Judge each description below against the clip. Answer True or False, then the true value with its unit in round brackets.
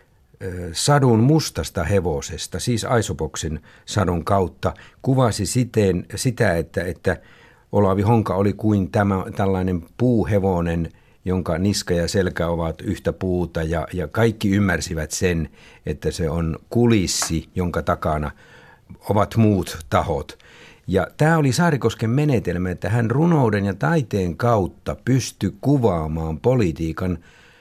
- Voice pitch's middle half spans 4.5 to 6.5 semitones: True (5.2 semitones)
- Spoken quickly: False (115 wpm)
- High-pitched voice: False (95 Hz)